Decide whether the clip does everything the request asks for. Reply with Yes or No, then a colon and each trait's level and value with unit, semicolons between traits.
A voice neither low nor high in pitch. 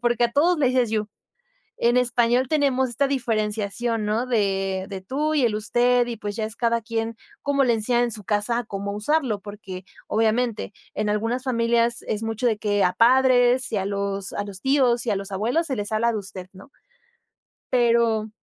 No: high, 230 Hz